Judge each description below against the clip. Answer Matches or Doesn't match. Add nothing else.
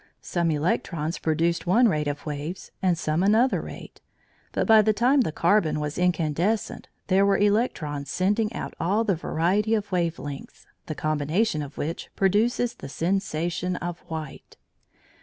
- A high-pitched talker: Doesn't match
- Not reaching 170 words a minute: Matches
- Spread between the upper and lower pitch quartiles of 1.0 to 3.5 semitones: Doesn't match